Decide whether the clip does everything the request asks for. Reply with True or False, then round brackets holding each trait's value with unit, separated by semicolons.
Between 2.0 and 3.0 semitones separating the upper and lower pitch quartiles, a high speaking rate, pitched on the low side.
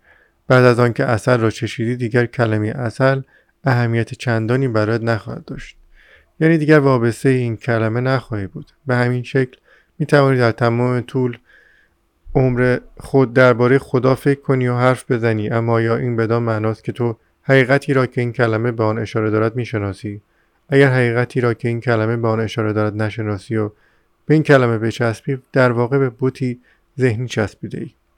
True (2.4 semitones; 165 wpm; 120 Hz)